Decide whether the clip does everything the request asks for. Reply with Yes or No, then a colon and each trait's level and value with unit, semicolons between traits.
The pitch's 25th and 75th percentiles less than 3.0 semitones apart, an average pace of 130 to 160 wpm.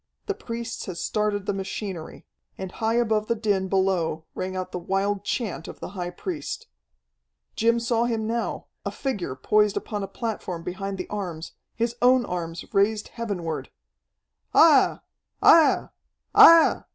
No: average, 4.0 semitones; average, 150 wpm